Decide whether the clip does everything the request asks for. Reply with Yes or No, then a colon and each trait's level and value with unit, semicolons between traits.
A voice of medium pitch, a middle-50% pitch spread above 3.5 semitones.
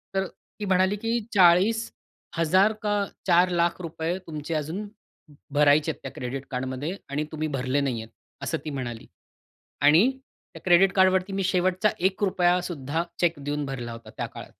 Yes: medium, 170 Hz; average, 4.8 semitones